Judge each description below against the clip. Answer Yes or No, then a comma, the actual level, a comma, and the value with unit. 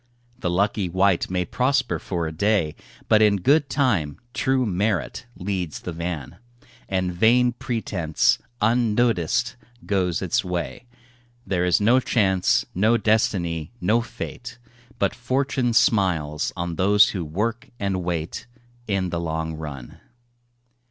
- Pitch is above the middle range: No, low, 100 Hz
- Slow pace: Yes, slow, 130 wpm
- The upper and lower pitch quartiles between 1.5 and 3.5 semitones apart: No, average, 5.2 semitones